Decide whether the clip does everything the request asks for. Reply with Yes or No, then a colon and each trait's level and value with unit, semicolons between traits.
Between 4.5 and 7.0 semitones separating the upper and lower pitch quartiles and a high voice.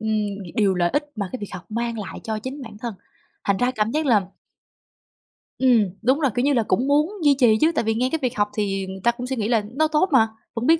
No: average, 4.1 semitones; high, 235 Hz